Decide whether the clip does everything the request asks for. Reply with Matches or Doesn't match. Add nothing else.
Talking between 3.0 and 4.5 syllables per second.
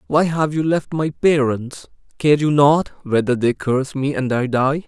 Matches